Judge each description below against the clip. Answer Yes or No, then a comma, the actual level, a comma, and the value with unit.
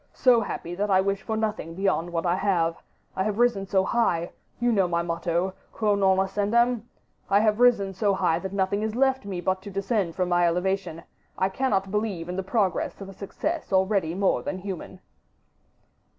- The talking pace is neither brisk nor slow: Yes, average, 195 wpm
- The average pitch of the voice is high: Yes, high, 195 Hz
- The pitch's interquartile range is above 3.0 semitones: No, narrow, 2.5 semitones